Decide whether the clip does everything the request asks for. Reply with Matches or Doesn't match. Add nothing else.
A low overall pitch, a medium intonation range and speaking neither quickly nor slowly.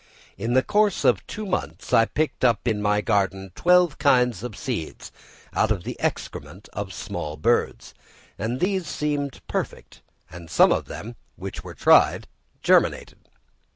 Doesn't match